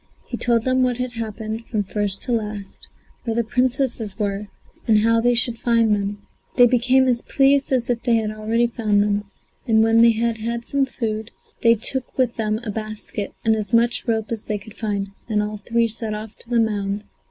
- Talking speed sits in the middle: No, fast, 210 wpm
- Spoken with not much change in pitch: Yes, narrow, 2.1 semitones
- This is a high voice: Yes, high, 225 Hz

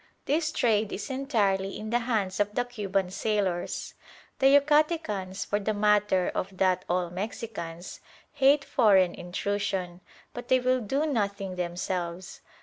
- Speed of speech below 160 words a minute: Yes, average, 140 wpm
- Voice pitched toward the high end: Yes, high, 205 Hz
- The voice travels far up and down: No, average, 4.7 semitones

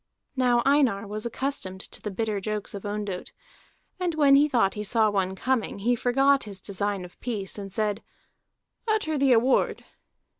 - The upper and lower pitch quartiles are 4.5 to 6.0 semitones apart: Yes, average, 4.8 semitones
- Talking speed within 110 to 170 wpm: Yes, average, 165 wpm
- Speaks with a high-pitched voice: Yes, high, 220 Hz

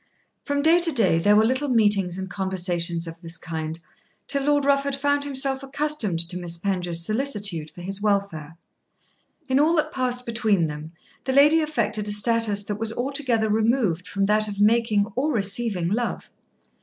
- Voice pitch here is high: Yes, high, 215 Hz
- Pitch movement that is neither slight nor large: No, wide, 6.8 semitones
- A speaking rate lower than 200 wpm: Yes, average, 170 wpm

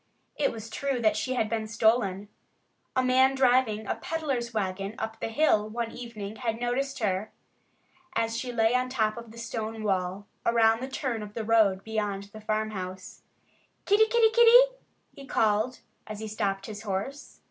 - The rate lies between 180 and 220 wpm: No, average, 170 wpm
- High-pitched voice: Yes, high, 225 Hz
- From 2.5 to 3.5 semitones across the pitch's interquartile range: Yes, average, 3.1 semitones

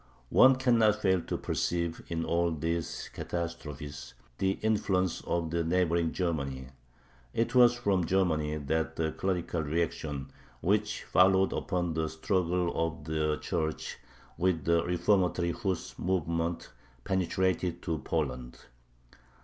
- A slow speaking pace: Yes, slow, 115 wpm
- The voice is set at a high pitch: No, very low, 85 Hz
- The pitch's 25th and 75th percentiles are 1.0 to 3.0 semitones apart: Yes, average, 2.7 semitones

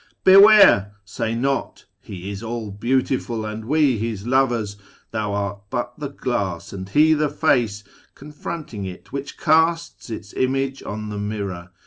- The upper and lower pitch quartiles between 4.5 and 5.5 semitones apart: Yes, average, 5.2 semitones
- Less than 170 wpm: Yes, average, 155 wpm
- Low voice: Yes, low, 115 Hz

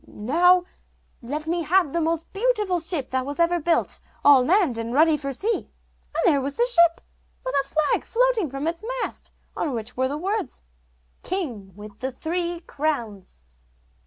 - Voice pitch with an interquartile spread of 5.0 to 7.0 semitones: Yes, average, 5.3 semitones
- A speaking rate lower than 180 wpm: Yes, average, 170 wpm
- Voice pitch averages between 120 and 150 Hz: No, very high, 315 Hz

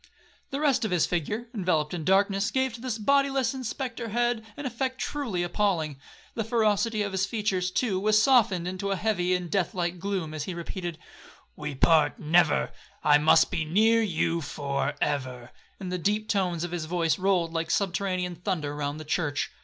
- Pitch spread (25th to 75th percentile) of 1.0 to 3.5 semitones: No, average, 4.9 semitones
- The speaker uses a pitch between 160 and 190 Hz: Yes, medium, 185 Hz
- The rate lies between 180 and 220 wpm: Yes, average, 185 wpm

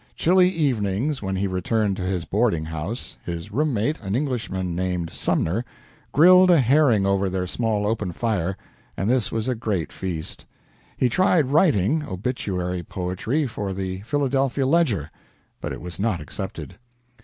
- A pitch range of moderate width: No, wide, 6.3 semitones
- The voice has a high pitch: No, low, 105 Hz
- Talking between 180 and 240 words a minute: No, average, 155 wpm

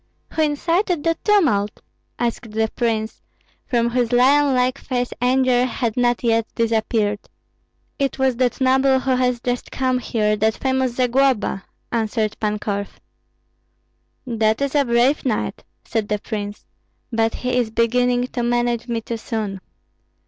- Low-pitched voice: No, high, 240 Hz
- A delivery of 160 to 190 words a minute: No, average, 145 wpm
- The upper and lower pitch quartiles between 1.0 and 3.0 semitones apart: Yes, average, 2.7 semitones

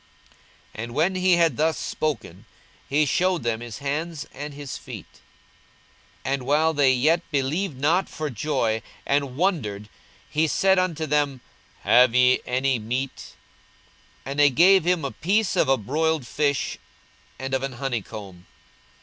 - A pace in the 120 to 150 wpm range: No, average, 160 wpm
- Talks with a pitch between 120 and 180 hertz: Yes, medium, 140 Hz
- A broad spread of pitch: No, average, 4.2 semitones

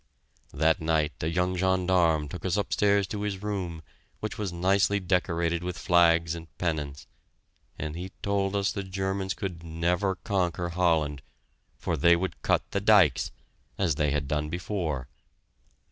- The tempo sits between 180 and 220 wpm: No, average, 150 wpm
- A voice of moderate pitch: No, very low, 90 Hz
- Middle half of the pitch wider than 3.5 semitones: No, average, 3.0 semitones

